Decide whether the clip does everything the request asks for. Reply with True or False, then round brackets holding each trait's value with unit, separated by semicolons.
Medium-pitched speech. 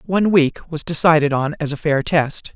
True (155 Hz)